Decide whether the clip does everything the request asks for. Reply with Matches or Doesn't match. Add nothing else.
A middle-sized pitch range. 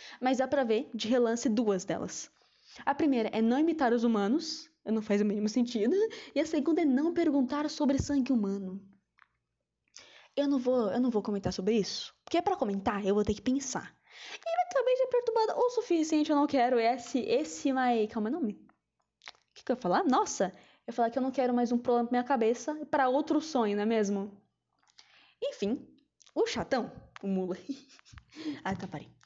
Doesn't match